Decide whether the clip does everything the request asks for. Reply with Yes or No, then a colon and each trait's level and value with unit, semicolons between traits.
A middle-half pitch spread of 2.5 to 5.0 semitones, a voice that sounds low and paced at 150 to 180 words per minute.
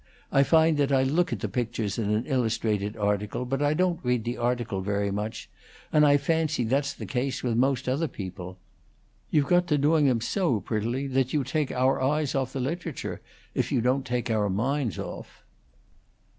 No: average, 4.4 semitones; low, 130 Hz; average, 190 wpm